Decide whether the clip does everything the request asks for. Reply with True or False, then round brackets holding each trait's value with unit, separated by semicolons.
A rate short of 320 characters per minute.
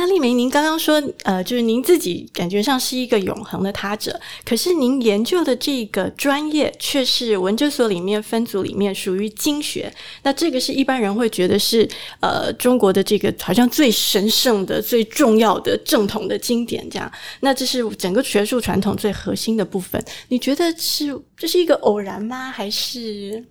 True (285 characters per minute)